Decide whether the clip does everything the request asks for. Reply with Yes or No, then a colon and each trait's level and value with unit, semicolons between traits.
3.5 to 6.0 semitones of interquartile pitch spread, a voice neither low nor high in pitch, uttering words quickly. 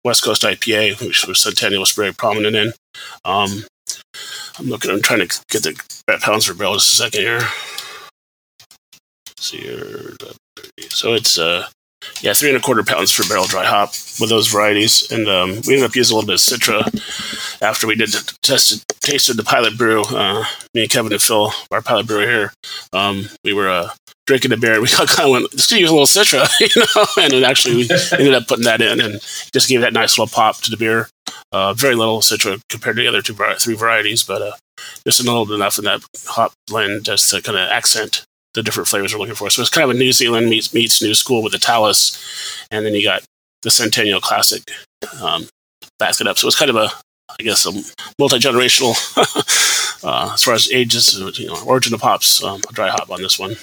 No: average, 4.1 semitones; low, 115 Hz; fast, 215 wpm